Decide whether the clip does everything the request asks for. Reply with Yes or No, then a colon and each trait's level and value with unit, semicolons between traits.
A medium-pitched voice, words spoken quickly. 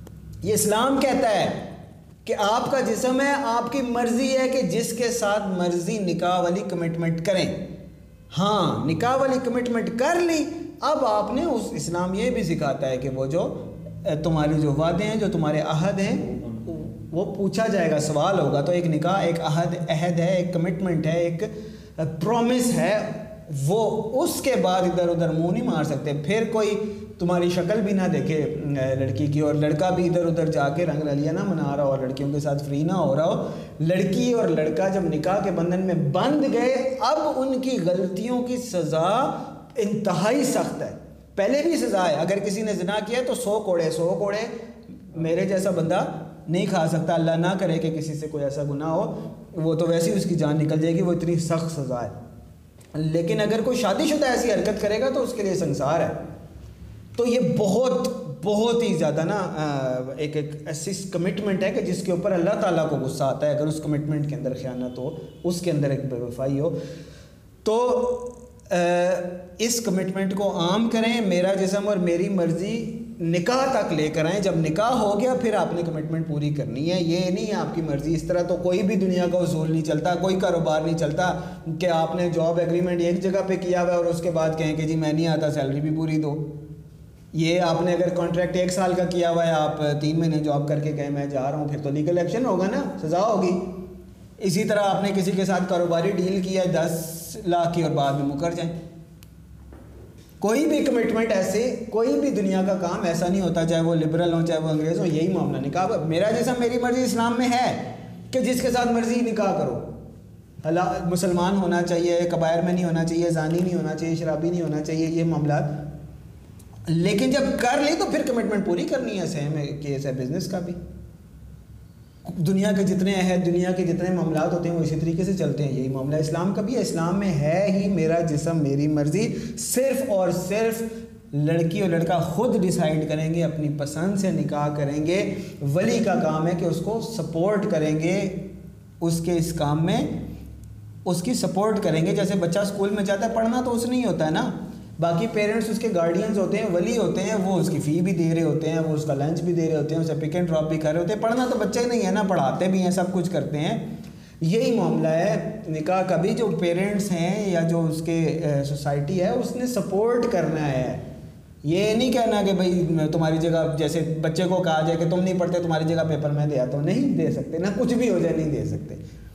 Yes: medium, 175 Hz; fast, 210 wpm